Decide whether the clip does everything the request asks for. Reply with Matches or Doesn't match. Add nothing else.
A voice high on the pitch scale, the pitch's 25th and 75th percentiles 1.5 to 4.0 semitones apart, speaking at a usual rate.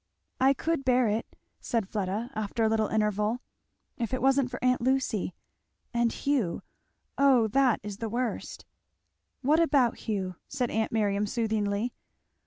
Matches